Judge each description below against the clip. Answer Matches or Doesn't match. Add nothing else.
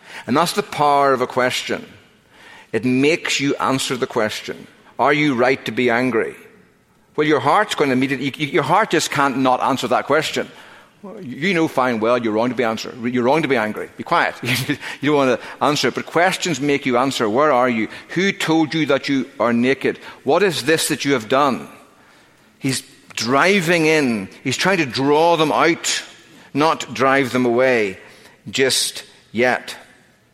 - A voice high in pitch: Doesn't match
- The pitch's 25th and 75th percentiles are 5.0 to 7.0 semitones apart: Doesn't match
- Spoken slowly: Doesn't match